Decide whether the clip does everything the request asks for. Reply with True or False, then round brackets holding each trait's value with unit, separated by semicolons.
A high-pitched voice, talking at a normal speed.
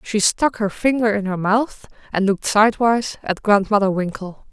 True (210 Hz; 175 wpm)